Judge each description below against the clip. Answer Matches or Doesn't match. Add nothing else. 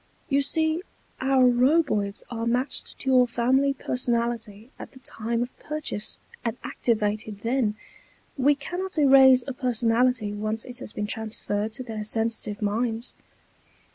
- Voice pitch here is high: Matches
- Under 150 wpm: Matches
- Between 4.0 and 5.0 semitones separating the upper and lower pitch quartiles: Doesn't match